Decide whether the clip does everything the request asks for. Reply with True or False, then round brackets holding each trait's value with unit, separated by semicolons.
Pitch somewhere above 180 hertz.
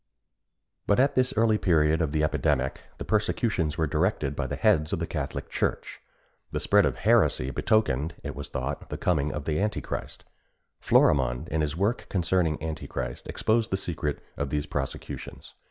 False (80 Hz)